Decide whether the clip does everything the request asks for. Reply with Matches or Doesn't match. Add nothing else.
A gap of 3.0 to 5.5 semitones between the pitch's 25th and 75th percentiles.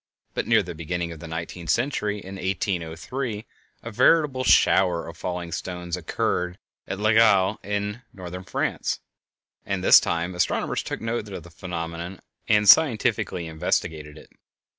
Matches